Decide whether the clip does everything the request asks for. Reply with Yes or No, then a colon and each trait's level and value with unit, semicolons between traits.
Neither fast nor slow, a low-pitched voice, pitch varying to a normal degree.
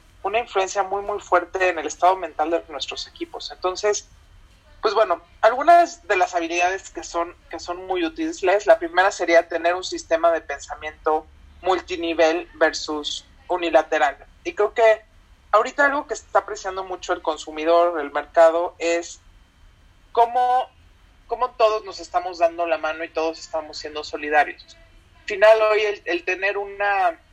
No: average, 150 wpm; medium, 175 Hz; average, 4.7 semitones